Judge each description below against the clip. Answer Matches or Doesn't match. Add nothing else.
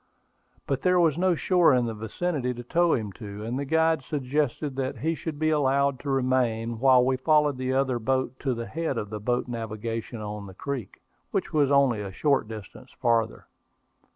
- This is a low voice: Matches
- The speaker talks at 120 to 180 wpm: Doesn't match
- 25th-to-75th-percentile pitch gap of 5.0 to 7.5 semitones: Doesn't match